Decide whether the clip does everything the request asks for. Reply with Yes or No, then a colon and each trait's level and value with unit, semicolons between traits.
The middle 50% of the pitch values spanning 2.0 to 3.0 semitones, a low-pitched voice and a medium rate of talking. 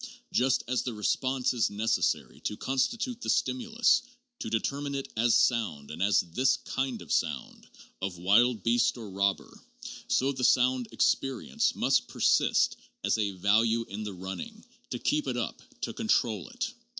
No: average, 4.6 semitones; low, 120 Hz; average, 160 wpm